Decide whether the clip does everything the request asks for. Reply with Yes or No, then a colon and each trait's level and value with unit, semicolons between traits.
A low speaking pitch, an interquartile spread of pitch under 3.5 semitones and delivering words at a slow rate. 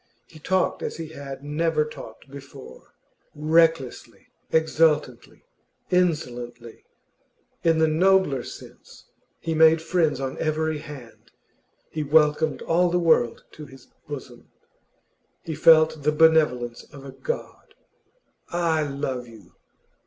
No: medium, 155 Hz; average, 3.1 semitones; slow, 115 wpm